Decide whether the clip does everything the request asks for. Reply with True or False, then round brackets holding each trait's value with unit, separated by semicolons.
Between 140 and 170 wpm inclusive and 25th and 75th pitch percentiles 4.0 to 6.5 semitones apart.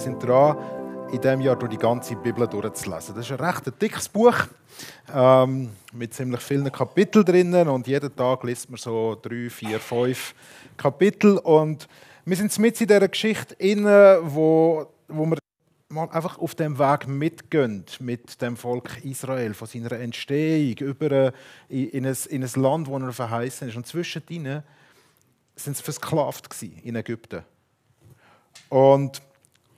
True (145 wpm; 4.5 semitones)